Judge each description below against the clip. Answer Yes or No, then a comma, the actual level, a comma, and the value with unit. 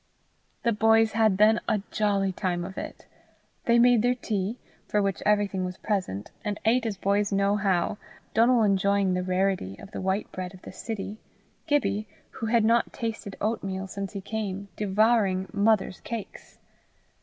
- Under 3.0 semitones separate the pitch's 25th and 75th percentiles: Yes, narrow, 2.6 semitones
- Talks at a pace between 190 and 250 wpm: No, average, 165 wpm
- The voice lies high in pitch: Yes, high, 205 Hz